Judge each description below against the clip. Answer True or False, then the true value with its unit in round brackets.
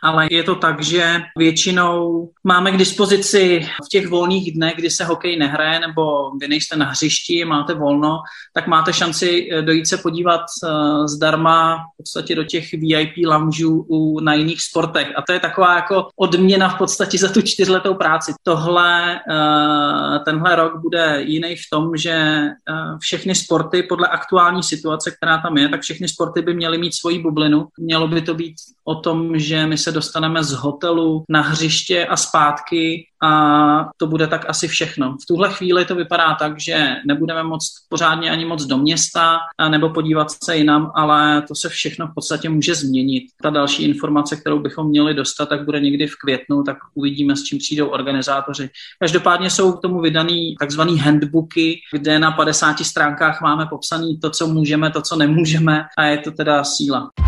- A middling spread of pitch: False (2.1 semitones)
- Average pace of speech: False (175 wpm)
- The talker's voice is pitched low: False (160 Hz)